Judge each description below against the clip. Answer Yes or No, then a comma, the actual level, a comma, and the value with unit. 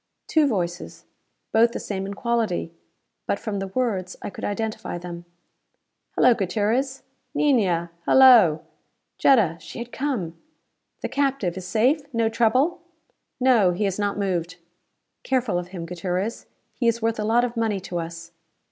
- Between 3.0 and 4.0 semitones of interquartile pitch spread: No, average, 5.2 semitones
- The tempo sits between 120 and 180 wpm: Yes, average, 150 wpm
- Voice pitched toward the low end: No, high, 210 Hz